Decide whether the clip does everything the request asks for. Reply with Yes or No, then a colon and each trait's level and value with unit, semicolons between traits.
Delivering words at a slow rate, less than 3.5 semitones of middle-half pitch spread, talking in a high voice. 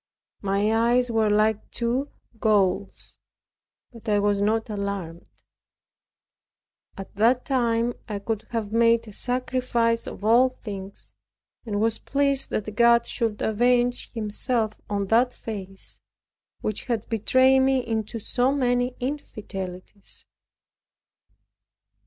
Yes: slow, 115 wpm; average, 3.0 semitones; high, 225 Hz